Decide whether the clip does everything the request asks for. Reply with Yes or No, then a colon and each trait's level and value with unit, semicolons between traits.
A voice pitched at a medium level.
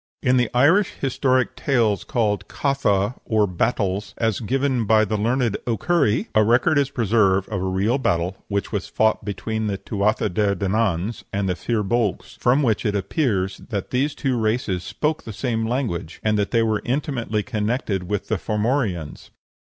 No: low, 110 Hz